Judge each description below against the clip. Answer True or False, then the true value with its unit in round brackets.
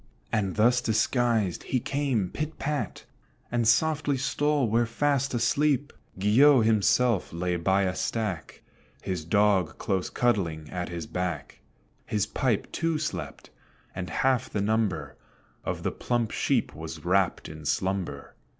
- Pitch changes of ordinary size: False (5.7 semitones)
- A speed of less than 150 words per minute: True (135 wpm)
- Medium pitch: False (110 Hz)